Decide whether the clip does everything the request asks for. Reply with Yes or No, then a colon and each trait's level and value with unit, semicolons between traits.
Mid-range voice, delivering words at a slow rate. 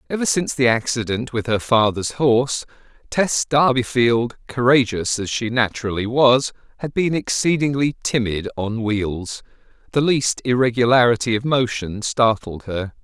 No: low, 120 Hz; slow, 130 wpm